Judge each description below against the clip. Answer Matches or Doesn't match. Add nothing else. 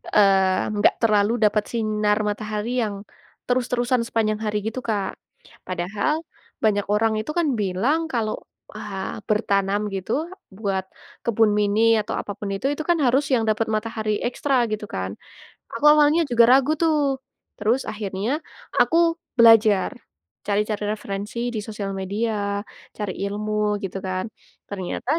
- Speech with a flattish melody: Matches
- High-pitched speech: Matches